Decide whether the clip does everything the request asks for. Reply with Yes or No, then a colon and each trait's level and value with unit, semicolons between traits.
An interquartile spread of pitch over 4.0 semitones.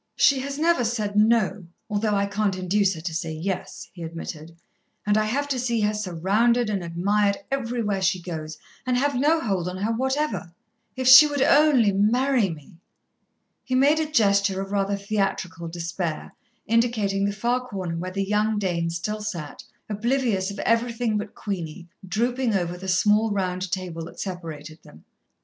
Yes: average, 4.5 semitones